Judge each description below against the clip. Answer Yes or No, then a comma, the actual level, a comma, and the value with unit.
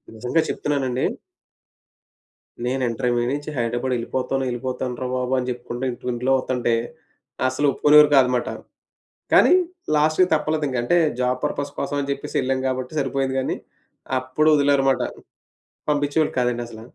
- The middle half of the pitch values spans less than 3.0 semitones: Yes, narrow, 2.4 semitones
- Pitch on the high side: No, low, 130 Hz